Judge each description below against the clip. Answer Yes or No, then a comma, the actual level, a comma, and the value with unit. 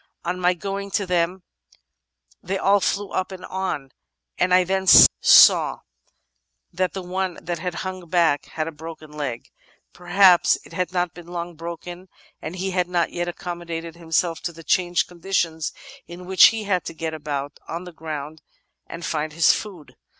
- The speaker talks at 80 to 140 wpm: No, average, 175 wpm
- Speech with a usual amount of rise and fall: No, narrow, 2.2 semitones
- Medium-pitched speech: Yes, medium, 175 Hz